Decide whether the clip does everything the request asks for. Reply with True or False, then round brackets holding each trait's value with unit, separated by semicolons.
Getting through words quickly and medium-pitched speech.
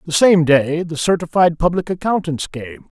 False (160 wpm; 165 Hz)